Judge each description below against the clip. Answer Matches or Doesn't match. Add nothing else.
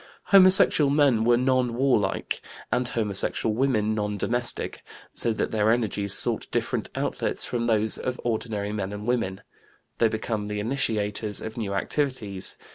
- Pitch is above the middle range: Doesn't match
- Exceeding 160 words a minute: Doesn't match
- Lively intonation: Doesn't match